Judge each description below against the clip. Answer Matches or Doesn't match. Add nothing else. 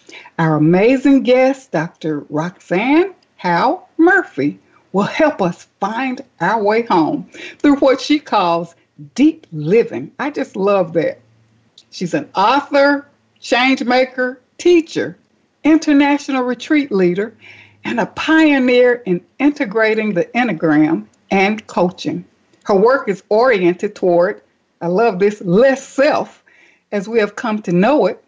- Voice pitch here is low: Doesn't match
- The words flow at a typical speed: Doesn't match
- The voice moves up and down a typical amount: Doesn't match